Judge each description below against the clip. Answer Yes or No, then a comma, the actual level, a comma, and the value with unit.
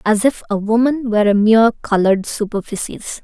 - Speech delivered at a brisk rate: No, average, 165 wpm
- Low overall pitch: No, high, 220 Hz